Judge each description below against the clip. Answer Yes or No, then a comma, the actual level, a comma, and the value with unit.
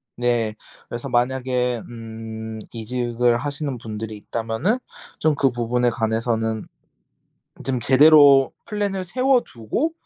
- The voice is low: Yes, low, 120 Hz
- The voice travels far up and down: No, average, 3.9 semitones